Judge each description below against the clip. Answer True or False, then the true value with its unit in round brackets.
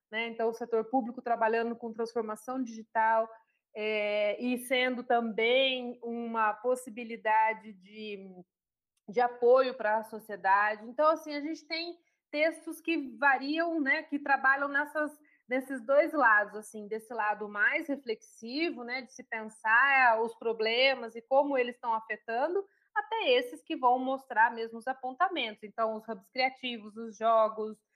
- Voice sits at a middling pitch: False (240 Hz)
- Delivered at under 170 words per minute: True (140 wpm)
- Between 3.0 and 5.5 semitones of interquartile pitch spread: True (3.8 semitones)